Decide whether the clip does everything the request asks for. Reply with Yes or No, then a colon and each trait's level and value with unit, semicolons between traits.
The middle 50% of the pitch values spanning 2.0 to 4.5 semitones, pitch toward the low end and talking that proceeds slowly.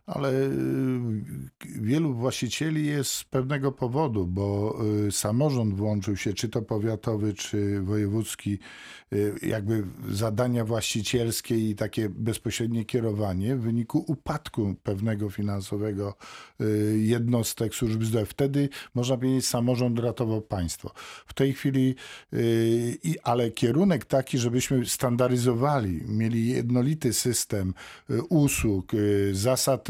Yes: average, 3.5 semitones; low, 115 Hz; slow, 100 wpm